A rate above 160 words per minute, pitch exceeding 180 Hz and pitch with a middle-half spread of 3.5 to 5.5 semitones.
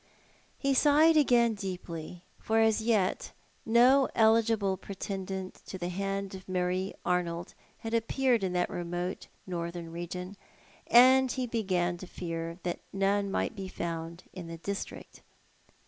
No: slow, 135 wpm; high, 190 Hz; average, 4.1 semitones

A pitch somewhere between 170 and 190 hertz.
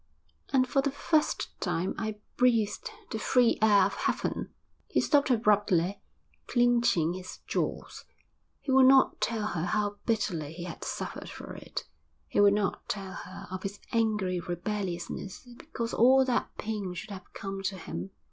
No: high, 205 Hz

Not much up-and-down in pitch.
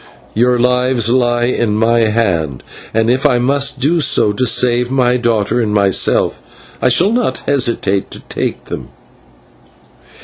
Yes: narrow, 2.3 semitones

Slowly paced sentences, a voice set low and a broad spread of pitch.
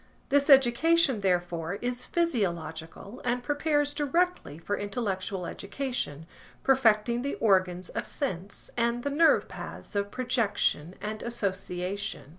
No: slow, 115 wpm; high, 220 Hz; wide, 6.2 semitones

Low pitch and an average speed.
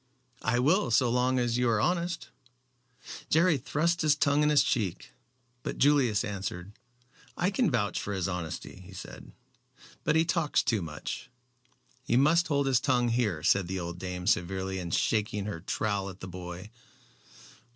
Yes: low, 115 Hz; average, 165 wpm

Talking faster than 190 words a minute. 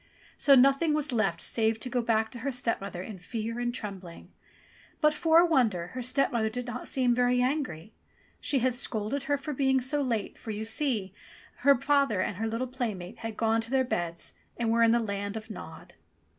Yes: average, 200 wpm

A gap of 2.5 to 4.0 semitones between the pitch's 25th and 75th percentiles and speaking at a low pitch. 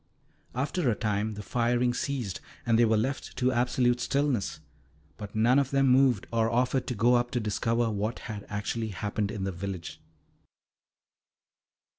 Yes: average, 3.0 semitones; low, 115 Hz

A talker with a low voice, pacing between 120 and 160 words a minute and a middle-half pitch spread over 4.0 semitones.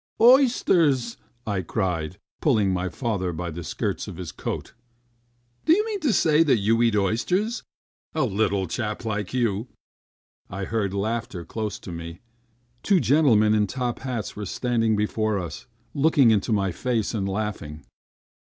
Yes: low, 110 Hz; average, 150 wpm; average, 4.7 semitones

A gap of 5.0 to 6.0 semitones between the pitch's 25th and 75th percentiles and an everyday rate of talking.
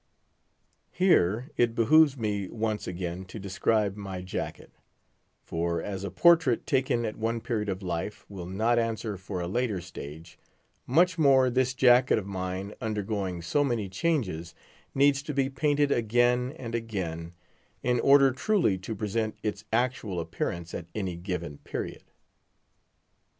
Yes: wide, 5.4 semitones; average, 145 wpm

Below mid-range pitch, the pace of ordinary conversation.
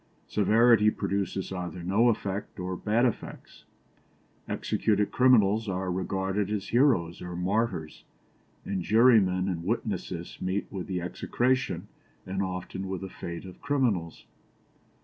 No: very low, 95 Hz; slow, 125 wpm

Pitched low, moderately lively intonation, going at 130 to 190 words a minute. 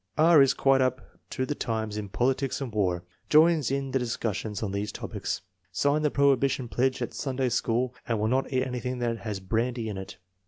No: low, 125 Hz; average, 3.5 semitones; average, 200 wpm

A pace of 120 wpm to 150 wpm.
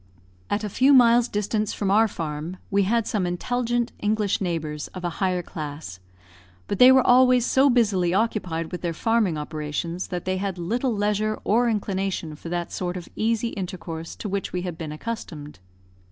No: average, 180 wpm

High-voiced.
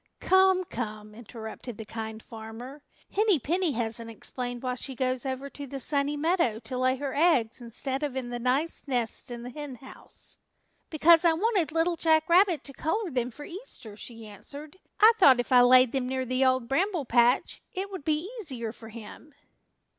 Yes: very high, 260 Hz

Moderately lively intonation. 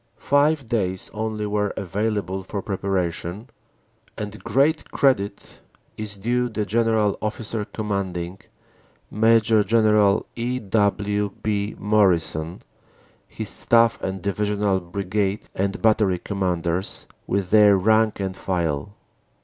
No: narrow, 2.3 semitones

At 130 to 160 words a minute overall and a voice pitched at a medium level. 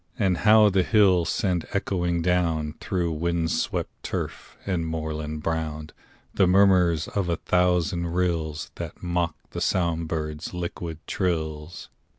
No: slow, 135 wpm; very low, 85 Hz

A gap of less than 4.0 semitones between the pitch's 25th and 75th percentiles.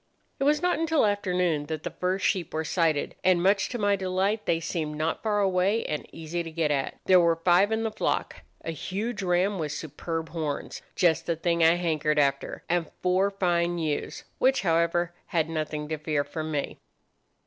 Yes: average, 3.3 semitones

